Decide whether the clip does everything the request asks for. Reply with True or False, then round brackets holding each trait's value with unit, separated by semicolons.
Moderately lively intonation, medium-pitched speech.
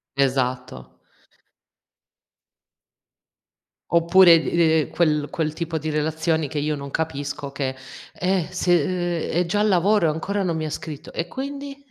True (3.1 semitones; 160 Hz)